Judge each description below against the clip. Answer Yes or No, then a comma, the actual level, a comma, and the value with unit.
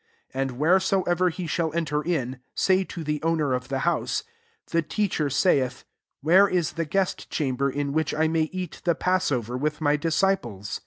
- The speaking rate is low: No, average, 180 wpm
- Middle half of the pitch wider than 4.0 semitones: Yes, average, 4.4 semitones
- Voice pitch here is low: No, medium, 160 Hz